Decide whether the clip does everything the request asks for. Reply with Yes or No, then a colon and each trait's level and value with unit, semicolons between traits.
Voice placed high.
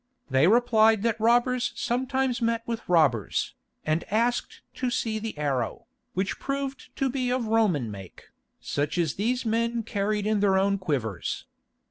Yes: high, 220 Hz